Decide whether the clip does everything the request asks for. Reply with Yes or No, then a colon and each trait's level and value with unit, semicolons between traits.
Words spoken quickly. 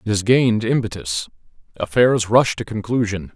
No: average, 145 wpm